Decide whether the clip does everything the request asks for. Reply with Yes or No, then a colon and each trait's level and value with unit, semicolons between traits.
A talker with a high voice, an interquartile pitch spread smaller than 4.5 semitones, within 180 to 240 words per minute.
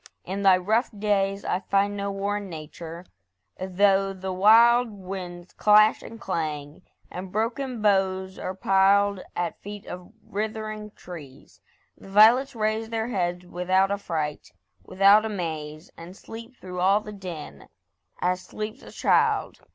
No: high, 195 Hz; average, 2.8 semitones; average, 140 wpm